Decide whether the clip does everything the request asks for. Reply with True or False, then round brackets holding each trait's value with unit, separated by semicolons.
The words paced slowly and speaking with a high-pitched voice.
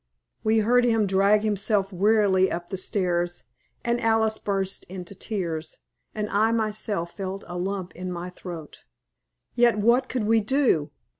False (150 wpm; 200 Hz)